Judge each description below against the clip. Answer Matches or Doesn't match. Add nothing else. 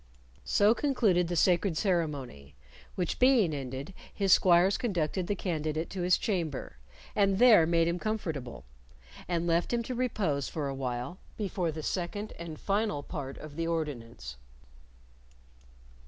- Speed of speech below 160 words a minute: Matches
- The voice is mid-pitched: Matches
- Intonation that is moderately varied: Matches